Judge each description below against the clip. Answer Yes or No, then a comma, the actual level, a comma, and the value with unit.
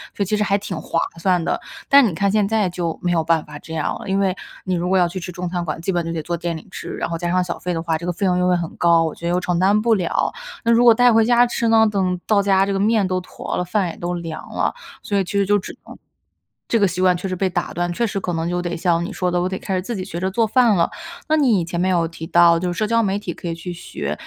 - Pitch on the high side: No, medium, 180 Hz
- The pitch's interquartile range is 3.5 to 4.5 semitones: No, average, 2.8 semitones